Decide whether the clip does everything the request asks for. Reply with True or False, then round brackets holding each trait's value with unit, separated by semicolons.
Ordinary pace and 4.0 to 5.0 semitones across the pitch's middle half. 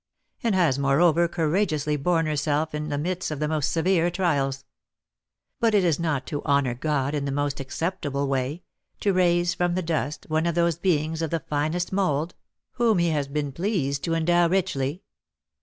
False (180 wpm; 3.2 semitones)